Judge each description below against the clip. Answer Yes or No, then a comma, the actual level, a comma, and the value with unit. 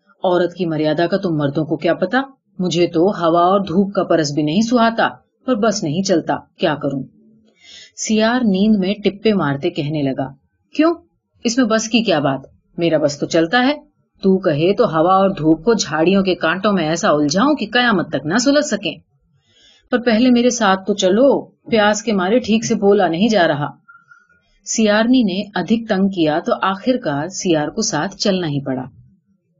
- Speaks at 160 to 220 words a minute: Yes, average, 185 wpm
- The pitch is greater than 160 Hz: Yes, high, 190 Hz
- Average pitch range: No, wide, 5.7 semitones